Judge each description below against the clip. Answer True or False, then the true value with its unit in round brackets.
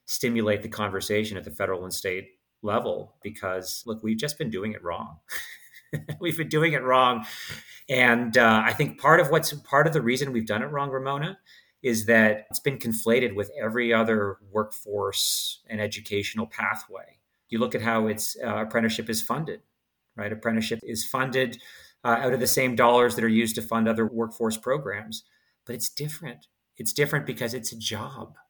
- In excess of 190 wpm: False (180 wpm)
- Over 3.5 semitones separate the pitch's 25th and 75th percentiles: False (3.1 semitones)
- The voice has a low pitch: True (115 Hz)